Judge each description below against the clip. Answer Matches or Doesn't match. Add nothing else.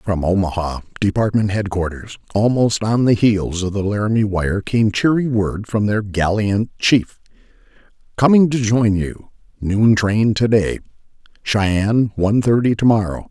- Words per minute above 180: Doesn't match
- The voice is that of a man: Matches